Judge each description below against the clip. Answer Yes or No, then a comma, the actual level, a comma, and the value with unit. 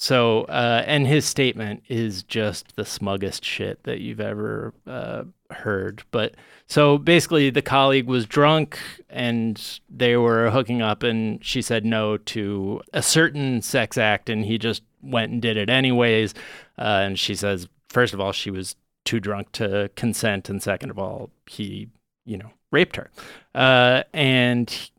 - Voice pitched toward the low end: Yes, low, 115 Hz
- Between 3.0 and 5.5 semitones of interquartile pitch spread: Yes, average, 3.6 semitones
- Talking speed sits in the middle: Yes, average, 165 wpm